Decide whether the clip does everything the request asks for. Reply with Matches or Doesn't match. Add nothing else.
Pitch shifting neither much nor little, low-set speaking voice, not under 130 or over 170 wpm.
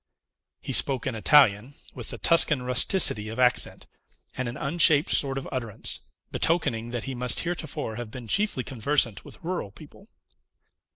Matches